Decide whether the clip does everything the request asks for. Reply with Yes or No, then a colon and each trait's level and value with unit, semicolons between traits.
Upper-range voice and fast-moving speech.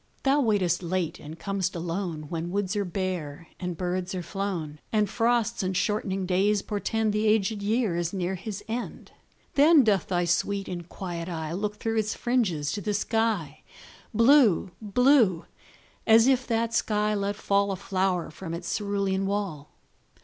No: high, 195 Hz; average, 165 wpm